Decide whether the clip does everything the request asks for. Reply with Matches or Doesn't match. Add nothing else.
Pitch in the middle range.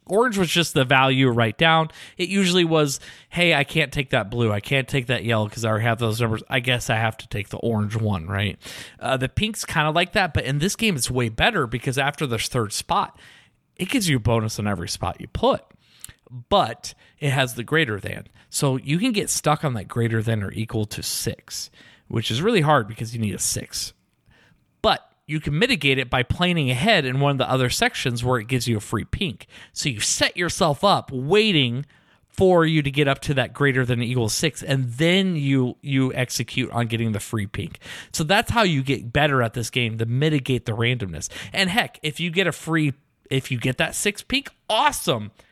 Doesn't match